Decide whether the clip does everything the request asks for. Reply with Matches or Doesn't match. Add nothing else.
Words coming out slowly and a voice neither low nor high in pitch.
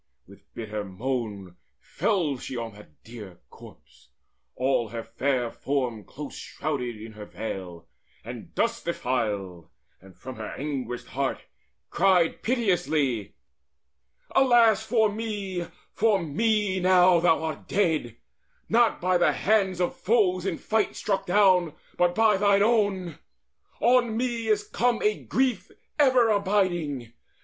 Matches